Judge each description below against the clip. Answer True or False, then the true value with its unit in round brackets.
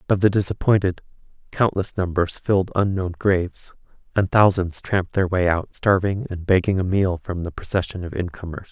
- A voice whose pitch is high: False (95 Hz)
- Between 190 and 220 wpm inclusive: False (165 wpm)